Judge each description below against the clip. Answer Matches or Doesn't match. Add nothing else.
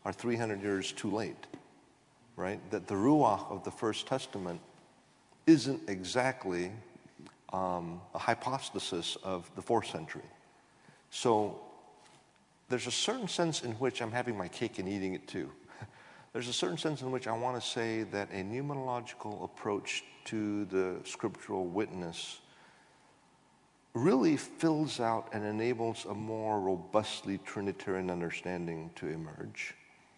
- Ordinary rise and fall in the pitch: Matches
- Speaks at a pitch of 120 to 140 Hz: Doesn't match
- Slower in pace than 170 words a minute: Matches